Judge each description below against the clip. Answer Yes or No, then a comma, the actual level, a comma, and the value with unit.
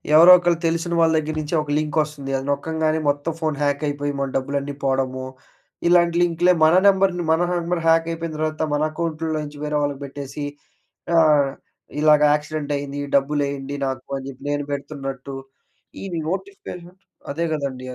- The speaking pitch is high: No, medium, 150 Hz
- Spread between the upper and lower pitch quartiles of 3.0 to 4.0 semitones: No, narrow, 2.6 semitones